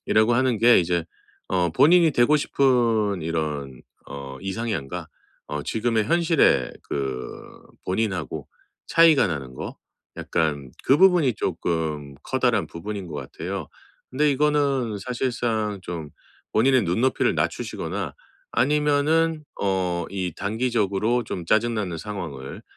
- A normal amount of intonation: No, wide, 7.6 semitones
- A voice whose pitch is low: Yes, low, 105 Hz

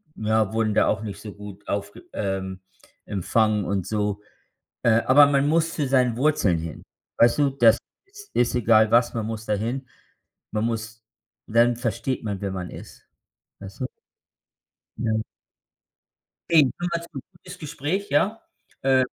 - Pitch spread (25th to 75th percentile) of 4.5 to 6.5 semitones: Yes, average, 4.8 semitones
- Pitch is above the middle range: No, low, 115 Hz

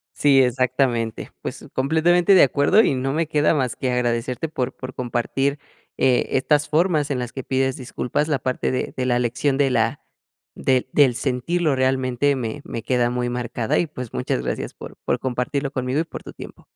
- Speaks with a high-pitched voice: No, low, 130 Hz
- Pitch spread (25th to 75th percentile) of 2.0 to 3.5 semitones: Yes, narrow, 2.6 semitones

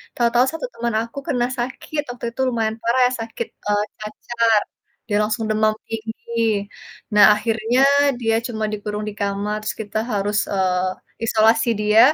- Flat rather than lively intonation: Yes, narrow, 2.0 semitones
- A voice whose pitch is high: Yes, high, 220 Hz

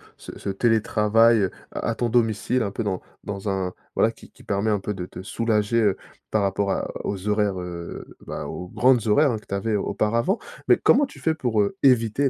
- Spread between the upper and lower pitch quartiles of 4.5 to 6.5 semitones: No, average, 2.8 semitones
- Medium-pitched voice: No, low, 105 Hz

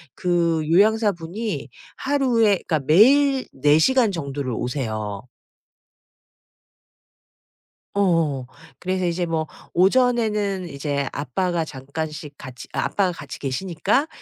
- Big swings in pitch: Yes, wide, 6.4 semitones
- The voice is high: No, medium, 170 Hz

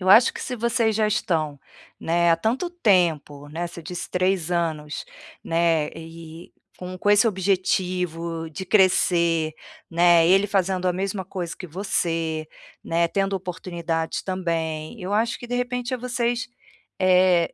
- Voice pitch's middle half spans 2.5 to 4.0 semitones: Yes, average, 3.2 semitones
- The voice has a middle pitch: Yes, medium, 180 Hz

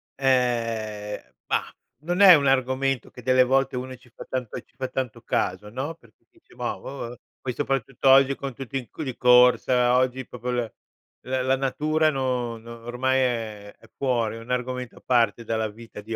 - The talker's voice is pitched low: Yes, low, 125 Hz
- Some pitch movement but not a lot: No, narrow, 2.2 semitones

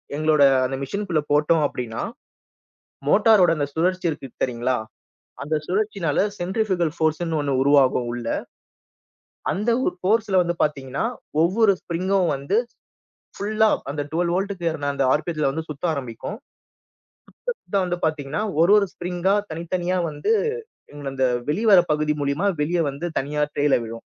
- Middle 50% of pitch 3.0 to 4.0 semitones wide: No, average, 4.4 semitones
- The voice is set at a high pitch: No, medium, 160 Hz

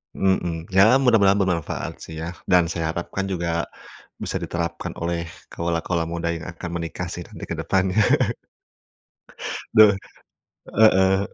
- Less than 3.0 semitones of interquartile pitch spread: Yes, narrow, 2.4 semitones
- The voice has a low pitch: Yes, very low, 90 Hz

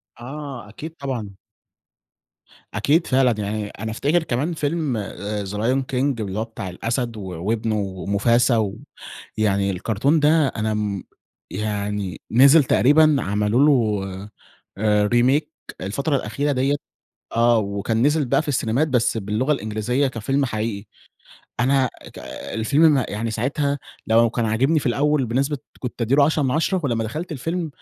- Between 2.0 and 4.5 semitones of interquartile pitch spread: No, average, 5.0 semitones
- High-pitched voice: No, low, 120 Hz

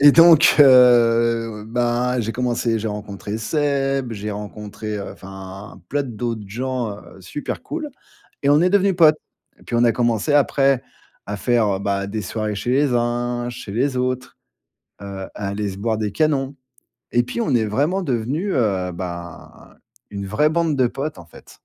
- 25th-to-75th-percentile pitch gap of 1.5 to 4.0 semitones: No, average, 4.7 semitones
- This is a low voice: Yes, low, 120 Hz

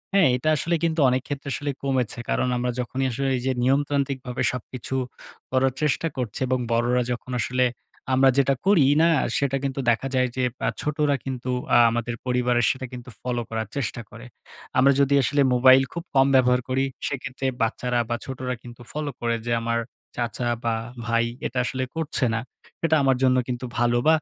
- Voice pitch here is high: No, low, 130 Hz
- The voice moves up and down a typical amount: No, narrow, 2.1 semitones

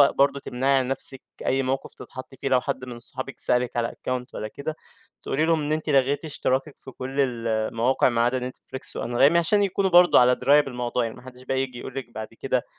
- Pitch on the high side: No, low, 130 Hz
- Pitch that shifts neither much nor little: No, narrow, 2.2 semitones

